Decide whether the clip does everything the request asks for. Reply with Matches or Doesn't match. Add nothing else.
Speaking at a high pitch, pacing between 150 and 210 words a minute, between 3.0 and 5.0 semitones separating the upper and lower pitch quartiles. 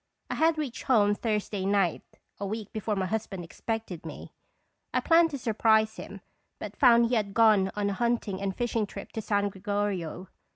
Doesn't match